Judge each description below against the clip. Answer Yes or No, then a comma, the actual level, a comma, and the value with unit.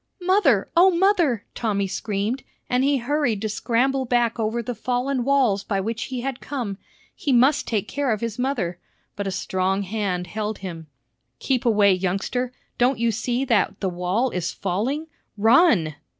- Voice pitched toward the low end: No, high, 230 Hz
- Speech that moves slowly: No, average, 165 wpm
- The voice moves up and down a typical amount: Yes, average, 4.8 semitones